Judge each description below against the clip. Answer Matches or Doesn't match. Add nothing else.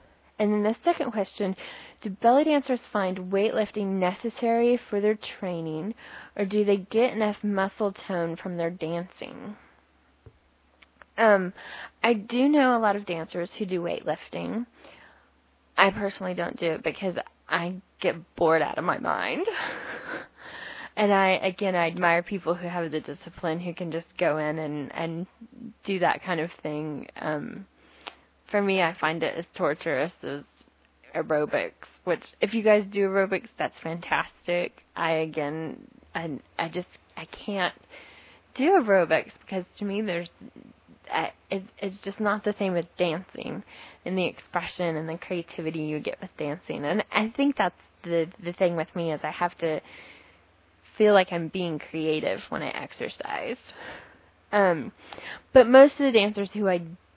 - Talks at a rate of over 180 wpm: Doesn't match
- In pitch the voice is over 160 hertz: Matches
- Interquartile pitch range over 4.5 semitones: Doesn't match